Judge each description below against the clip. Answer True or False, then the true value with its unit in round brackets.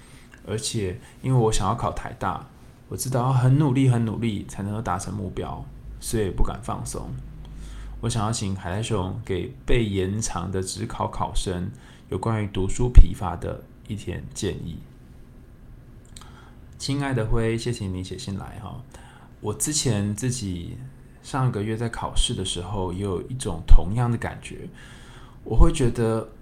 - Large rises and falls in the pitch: False (3.9 semitones)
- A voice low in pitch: True (110 Hz)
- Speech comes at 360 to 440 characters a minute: False (225 characters per minute)